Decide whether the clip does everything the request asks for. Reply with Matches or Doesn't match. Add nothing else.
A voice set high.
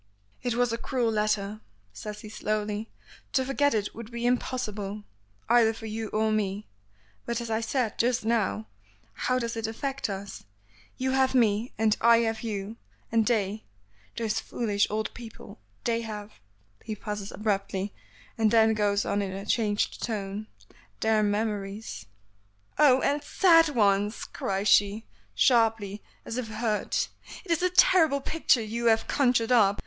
Matches